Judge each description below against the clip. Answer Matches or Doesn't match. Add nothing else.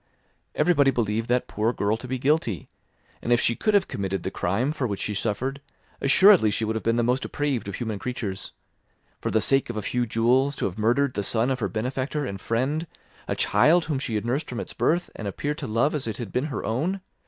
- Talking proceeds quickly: Matches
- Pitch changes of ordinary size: Matches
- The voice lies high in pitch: Doesn't match